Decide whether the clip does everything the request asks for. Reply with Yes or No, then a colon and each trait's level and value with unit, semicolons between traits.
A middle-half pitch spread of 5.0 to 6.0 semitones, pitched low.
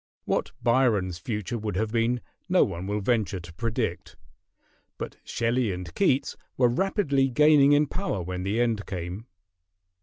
Yes: wide, 5.6 semitones; low, 115 Hz